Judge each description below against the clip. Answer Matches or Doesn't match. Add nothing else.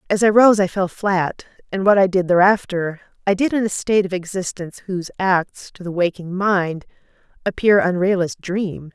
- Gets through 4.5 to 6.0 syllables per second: Matches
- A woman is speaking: Matches